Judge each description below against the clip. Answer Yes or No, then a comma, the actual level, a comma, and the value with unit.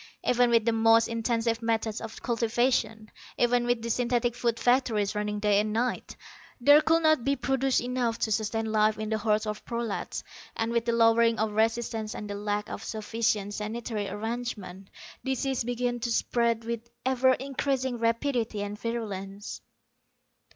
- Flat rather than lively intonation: Yes, narrow, 2.1 semitones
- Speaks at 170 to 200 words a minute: No, average, 160 wpm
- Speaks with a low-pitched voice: No, high, 230 Hz